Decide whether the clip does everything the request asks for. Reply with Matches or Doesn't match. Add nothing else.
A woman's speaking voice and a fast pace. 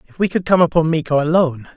Doesn't match